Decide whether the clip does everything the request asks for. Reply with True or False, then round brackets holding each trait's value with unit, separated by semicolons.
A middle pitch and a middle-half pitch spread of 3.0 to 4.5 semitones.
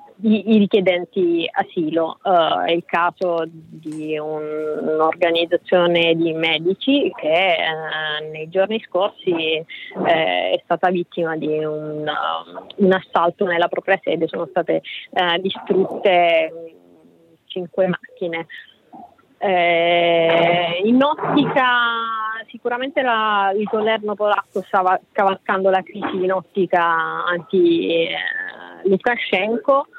True (180 Hz; 4.0 semitones)